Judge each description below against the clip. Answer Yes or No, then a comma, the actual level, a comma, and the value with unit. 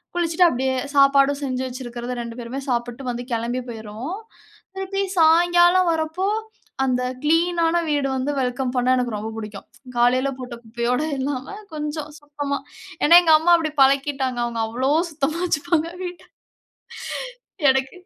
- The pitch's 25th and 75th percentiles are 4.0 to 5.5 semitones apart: Yes, average, 4.6 semitones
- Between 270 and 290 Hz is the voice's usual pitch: Yes, very high, 275 Hz